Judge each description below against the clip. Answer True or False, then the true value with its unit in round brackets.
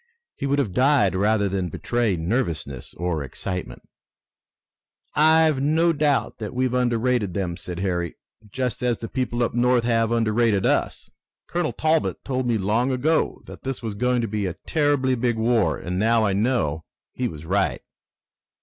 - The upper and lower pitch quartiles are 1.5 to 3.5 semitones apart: False (4.9 semitones)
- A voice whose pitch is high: False (115 Hz)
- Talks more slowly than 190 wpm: True (165 wpm)